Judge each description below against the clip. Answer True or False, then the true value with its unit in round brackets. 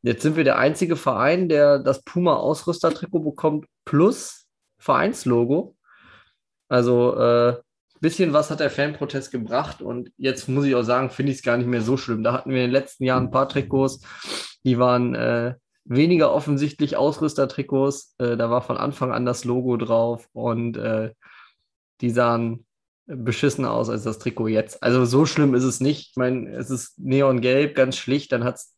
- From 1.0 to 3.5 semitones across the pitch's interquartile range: True (2.8 semitones)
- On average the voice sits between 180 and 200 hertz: False (130 Hz)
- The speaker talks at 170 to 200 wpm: True (175 wpm)